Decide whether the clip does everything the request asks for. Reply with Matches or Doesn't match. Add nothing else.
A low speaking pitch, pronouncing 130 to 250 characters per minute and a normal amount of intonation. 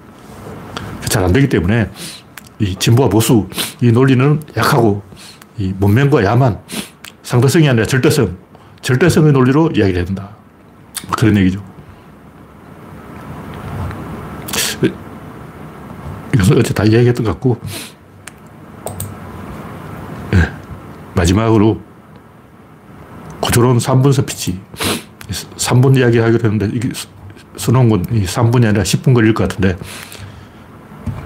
Matches